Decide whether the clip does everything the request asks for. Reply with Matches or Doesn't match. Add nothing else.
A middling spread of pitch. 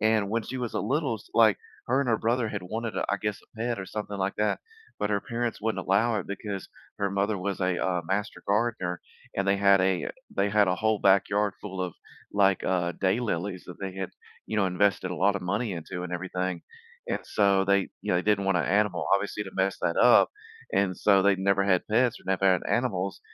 Doesn't match